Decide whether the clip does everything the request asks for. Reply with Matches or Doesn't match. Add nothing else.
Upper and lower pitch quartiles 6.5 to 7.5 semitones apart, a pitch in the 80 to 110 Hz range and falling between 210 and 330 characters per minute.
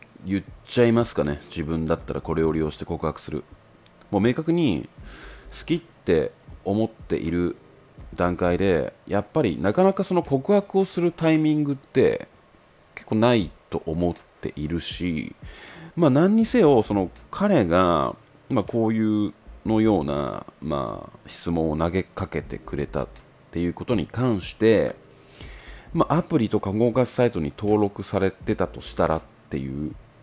Matches